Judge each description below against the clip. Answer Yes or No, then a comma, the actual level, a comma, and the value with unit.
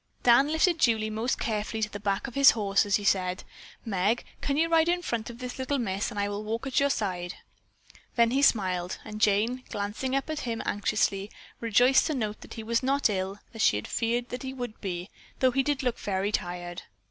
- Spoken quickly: Yes, fast, 210 wpm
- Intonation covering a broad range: No, average, 4.3 semitones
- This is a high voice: Yes, high, 225 Hz